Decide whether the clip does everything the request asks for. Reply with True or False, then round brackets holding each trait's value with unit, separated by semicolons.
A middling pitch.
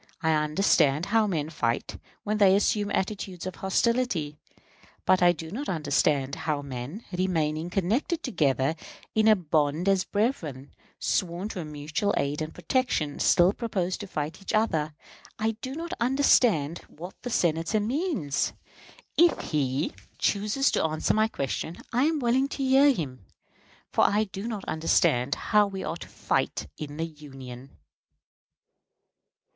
True (180 Hz)